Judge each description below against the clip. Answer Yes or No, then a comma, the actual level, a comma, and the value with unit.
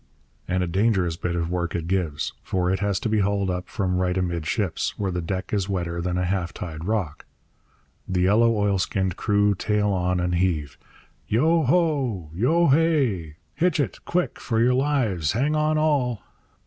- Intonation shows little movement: No, average, 4.8 semitones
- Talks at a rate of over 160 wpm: Yes, average, 175 wpm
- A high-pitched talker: No, very low, 95 Hz